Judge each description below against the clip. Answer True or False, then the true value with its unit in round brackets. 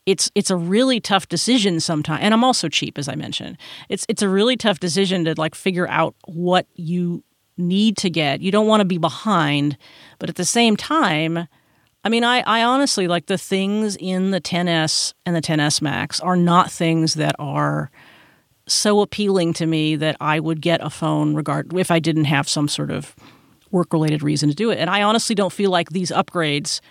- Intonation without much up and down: False (4.2 semitones)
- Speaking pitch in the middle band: True (175 Hz)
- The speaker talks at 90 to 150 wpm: False (205 wpm)